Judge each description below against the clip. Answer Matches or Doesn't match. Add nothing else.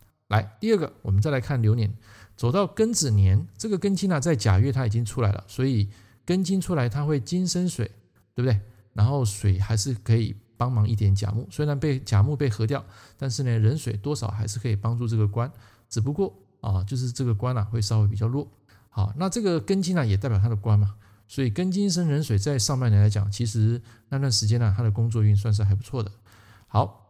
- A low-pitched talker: Matches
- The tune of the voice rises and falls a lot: Doesn't match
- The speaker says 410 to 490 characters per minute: Doesn't match